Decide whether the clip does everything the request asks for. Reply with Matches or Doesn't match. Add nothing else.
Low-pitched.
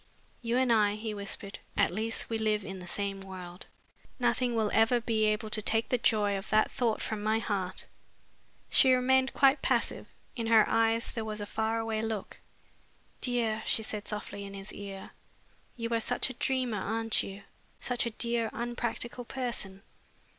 Doesn't match